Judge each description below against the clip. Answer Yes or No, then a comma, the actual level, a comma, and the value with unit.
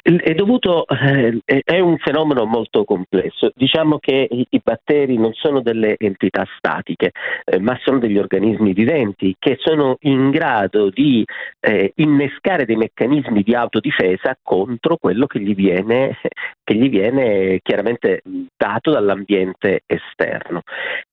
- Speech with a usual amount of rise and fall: No, wide, 6.5 semitones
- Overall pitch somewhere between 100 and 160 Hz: Yes, low, 135 Hz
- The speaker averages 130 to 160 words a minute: Yes, average, 135 wpm